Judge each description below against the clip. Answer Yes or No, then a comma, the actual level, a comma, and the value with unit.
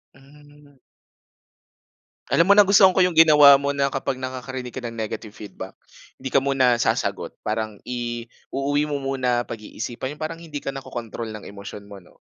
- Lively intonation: No, average, 3.8 semitones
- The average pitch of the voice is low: Yes, low, 130 Hz